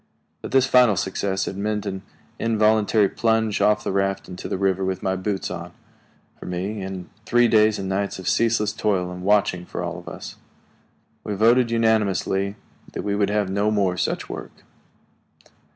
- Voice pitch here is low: Yes, low, 100 Hz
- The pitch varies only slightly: Yes, narrow, 2.2 semitones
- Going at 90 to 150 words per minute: No, average, 175 wpm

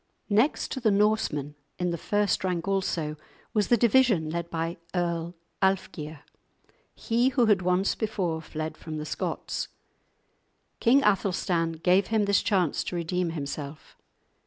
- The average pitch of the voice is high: No, medium, 180 Hz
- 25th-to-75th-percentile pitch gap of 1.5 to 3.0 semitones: No, average, 4.2 semitones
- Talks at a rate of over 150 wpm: No, average, 140 wpm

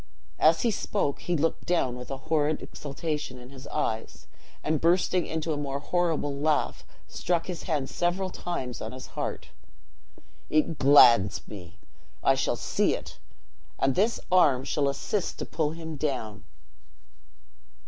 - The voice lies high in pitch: No, medium, 150 Hz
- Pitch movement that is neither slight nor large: Yes, average, 3.9 semitones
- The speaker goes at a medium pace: Yes, average, 150 wpm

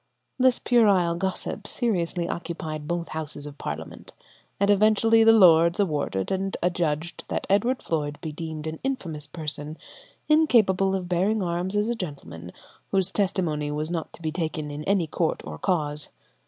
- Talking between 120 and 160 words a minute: Yes, average, 155 wpm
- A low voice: No, medium, 170 Hz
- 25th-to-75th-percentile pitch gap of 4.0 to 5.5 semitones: Yes, average, 4.5 semitones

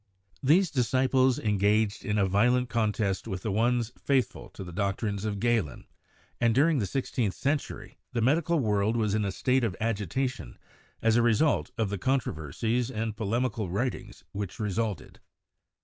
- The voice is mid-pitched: No, low, 115 Hz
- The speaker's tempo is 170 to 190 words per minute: No, average, 155 wpm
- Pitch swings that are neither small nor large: Yes, average, 3.8 semitones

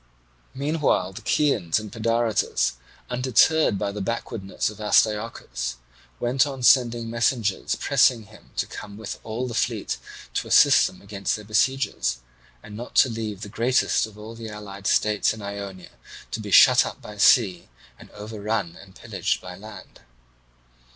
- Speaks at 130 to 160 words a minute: Yes, average, 150 wpm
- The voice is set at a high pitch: No, low, 110 Hz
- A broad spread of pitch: No, average, 2.8 semitones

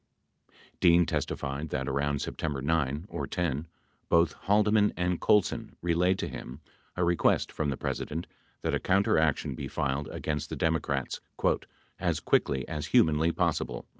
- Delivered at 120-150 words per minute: Yes, average, 140 wpm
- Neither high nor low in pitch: No, very low, 80 Hz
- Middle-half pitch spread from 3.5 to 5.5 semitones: Yes, average, 3.8 semitones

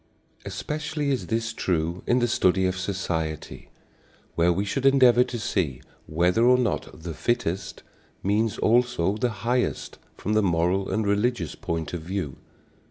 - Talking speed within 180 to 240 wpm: No, average, 150 wpm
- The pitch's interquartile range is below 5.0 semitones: No, wide, 5.6 semitones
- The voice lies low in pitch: Yes, low, 100 Hz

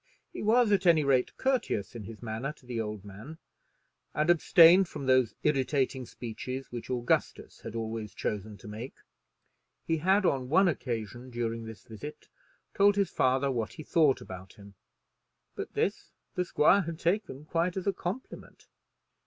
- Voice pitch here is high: No, low, 130 Hz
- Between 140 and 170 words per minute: Yes, average, 160 wpm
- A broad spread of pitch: Yes, wide, 6.9 semitones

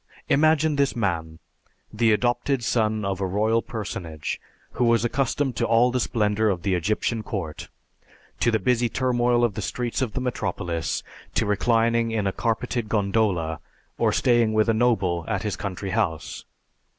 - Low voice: Yes, low, 110 Hz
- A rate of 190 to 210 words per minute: No, average, 165 wpm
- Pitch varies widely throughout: No, average, 3.6 semitones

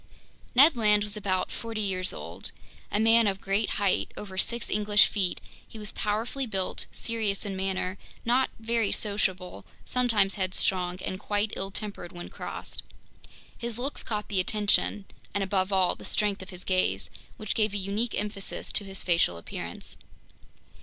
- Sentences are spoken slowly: No, average, 155 wpm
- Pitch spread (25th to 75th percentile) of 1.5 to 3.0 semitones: Yes, narrow, 2.4 semitones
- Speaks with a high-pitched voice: Yes, high, 205 Hz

